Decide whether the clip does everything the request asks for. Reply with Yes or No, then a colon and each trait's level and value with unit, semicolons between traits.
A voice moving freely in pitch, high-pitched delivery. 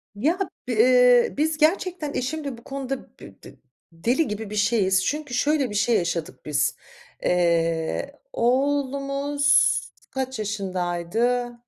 Yes: wide, 6.0 semitones; high, 245 Hz